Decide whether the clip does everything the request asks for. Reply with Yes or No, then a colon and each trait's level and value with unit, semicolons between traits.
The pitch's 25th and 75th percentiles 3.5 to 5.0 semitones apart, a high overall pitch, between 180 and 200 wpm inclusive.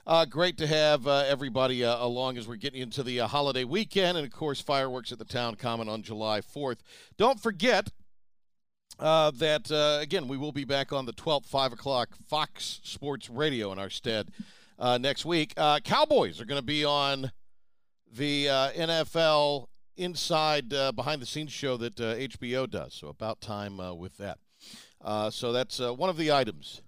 No: average, 4.2 semitones; low, 135 Hz; average, 190 wpm